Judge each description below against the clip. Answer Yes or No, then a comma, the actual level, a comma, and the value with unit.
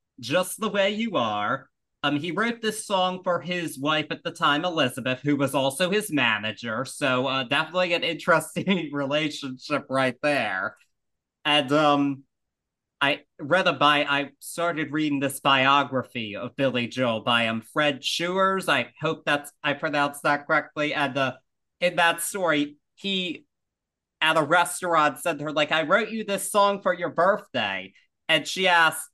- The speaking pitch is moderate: Yes, medium, 155 Hz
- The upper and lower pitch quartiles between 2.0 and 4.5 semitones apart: Yes, average, 4.2 semitones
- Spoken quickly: No, average, 165 wpm